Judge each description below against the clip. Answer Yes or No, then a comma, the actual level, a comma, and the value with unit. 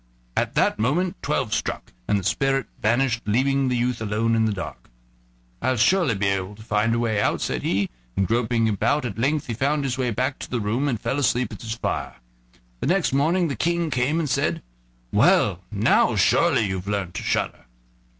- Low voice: Yes, low, 120 Hz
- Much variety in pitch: No, average, 4.3 semitones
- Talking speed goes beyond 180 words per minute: Yes, average, 200 wpm